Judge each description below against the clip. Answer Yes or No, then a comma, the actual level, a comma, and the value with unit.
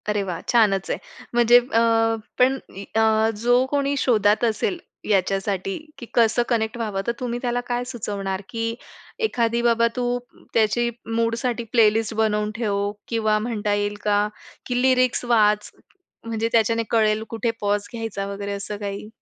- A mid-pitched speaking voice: No, high, 225 Hz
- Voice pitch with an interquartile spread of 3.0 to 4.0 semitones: No, narrow, 2.5 semitones